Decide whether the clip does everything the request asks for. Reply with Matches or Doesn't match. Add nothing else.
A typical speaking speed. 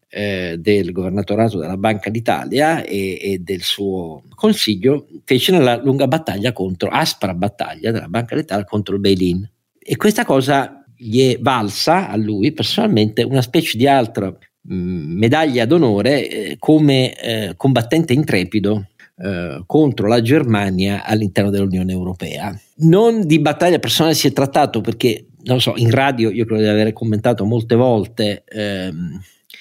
Matches